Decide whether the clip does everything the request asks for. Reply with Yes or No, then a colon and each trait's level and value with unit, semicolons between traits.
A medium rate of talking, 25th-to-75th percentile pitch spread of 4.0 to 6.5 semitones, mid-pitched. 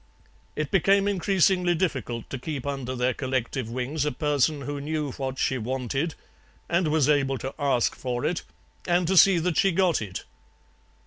Yes: average, 170 wpm; average, 4.8 semitones; medium, 145 Hz